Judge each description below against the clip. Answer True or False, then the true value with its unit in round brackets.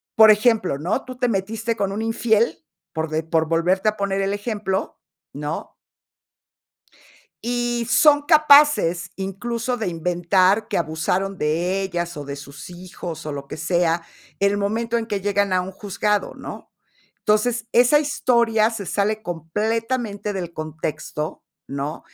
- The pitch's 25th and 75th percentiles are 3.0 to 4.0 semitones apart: False (4.8 semitones)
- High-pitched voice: True (200 Hz)